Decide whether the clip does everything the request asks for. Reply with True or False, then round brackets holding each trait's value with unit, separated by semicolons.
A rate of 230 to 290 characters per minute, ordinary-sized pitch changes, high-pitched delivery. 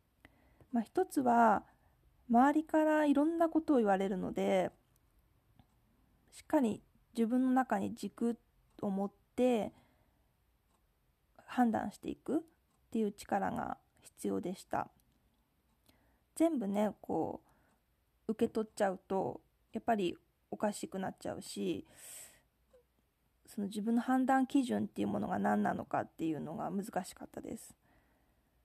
True (235 characters per minute; 5.0 semitones; 230 Hz)